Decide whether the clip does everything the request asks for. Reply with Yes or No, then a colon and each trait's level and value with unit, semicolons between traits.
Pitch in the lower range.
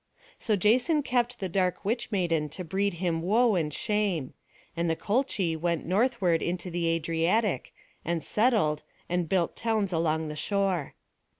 No: medium, 180 Hz